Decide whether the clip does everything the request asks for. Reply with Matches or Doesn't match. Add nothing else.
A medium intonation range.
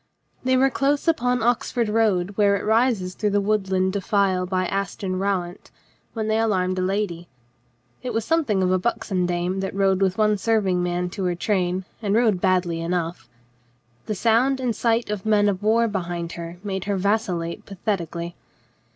Matches